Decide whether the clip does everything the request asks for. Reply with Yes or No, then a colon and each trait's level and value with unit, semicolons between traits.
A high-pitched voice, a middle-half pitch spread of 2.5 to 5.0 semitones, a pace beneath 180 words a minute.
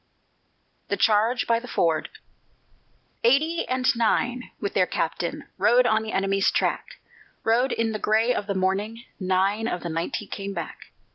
Yes: high, 215 Hz; average, 3.6 semitones; average, 155 wpm